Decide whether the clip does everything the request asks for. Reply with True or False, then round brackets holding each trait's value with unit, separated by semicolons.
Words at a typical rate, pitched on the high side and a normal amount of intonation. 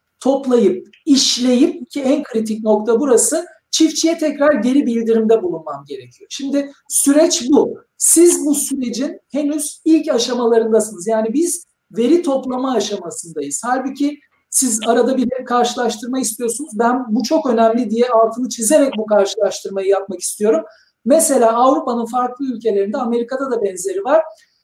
True (125 wpm; 255 Hz; 4.6 semitones)